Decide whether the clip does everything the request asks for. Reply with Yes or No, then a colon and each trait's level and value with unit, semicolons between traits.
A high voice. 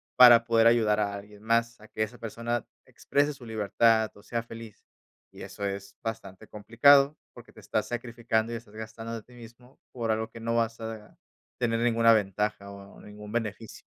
No: low, 115 Hz